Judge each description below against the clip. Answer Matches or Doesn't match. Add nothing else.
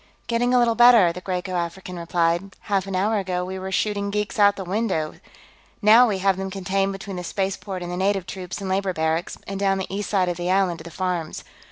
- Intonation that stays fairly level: Matches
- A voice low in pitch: Doesn't match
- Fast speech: Matches